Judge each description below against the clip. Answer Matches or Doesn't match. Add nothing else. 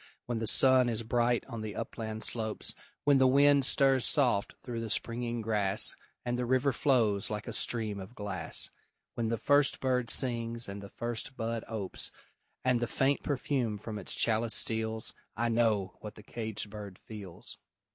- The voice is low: Matches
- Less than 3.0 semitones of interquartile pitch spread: Matches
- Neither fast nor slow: Matches